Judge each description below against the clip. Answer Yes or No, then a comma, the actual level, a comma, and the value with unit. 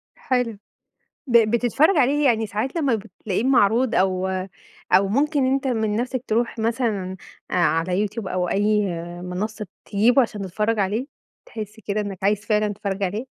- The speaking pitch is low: No, high, 215 Hz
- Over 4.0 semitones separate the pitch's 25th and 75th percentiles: No, average, 3.5 semitones